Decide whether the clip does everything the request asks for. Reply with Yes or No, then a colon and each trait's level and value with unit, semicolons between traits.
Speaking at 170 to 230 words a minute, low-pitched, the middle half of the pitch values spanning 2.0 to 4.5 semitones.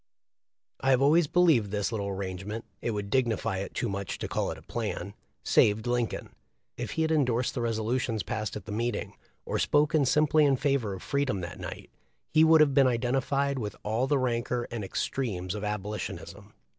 No: average, 200 wpm; low, 120 Hz; average, 4.9 semitones